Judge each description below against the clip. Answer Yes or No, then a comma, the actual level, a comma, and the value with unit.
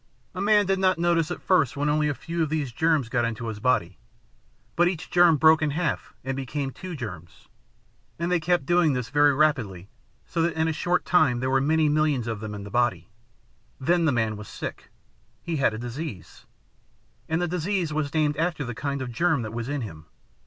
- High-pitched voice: No, medium, 150 Hz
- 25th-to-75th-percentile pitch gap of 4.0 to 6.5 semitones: Yes, average, 5.3 semitones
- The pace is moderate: No, fast, 215 wpm